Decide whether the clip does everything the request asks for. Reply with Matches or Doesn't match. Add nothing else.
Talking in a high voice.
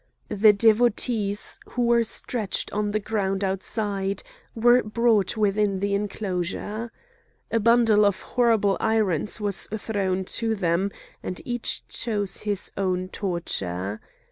Matches